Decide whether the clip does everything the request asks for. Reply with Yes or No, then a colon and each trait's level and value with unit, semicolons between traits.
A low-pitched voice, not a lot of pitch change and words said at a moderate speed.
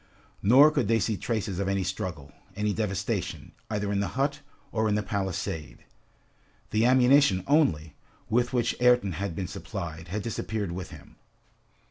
No: low, 105 Hz; average, 4.3 semitones; average, 155 wpm